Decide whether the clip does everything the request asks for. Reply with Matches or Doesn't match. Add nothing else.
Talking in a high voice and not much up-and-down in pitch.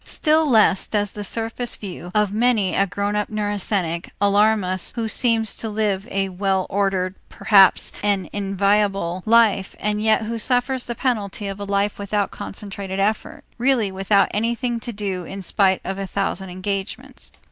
Matches